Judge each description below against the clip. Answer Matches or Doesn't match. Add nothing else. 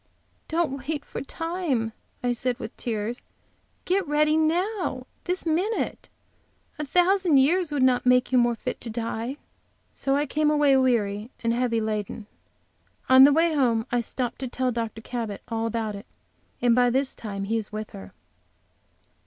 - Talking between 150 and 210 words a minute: Matches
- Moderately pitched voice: Doesn't match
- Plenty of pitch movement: Doesn't match